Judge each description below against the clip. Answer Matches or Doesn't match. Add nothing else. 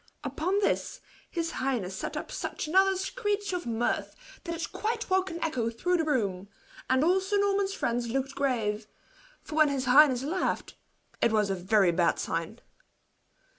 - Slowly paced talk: Doesn't match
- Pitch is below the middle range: Doesn't match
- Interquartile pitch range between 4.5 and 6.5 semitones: Doesn't match